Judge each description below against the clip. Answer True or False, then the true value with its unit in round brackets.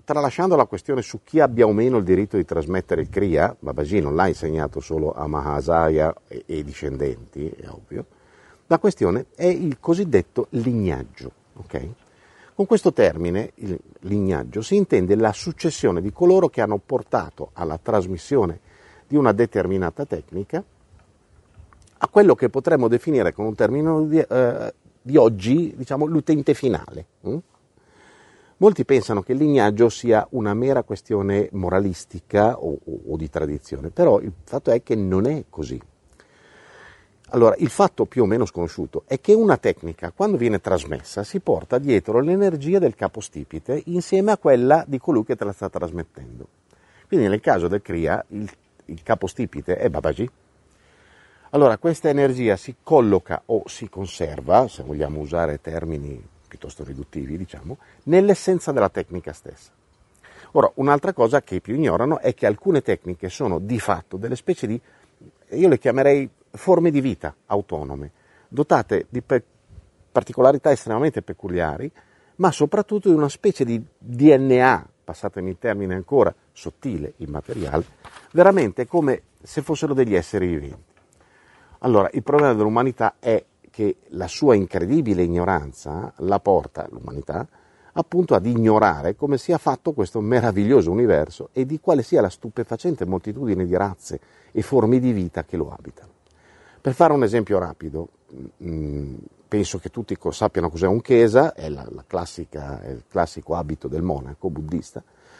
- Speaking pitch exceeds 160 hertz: False (110 Hz)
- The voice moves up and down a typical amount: False (8.3 semitones)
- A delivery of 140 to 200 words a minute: True (150 wpm)